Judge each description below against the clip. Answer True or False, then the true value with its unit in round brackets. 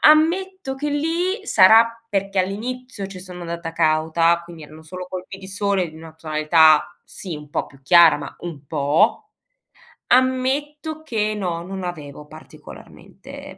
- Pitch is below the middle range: False (185 Hz)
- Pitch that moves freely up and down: True (7.9 semitones)